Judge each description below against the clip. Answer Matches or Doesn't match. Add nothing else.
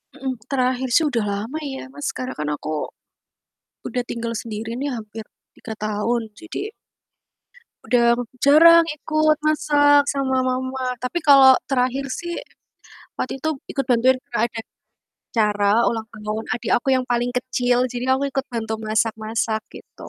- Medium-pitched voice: Doesn't match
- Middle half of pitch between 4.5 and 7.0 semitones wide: Doesn't match